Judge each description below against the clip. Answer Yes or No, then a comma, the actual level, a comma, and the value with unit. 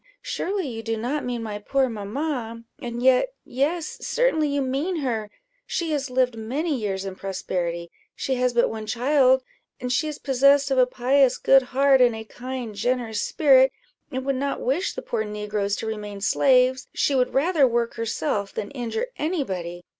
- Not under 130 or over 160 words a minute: No, average, 180 wpm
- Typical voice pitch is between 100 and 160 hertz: No, very high, 255 Hz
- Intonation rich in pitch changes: No, average, 3.9 semitones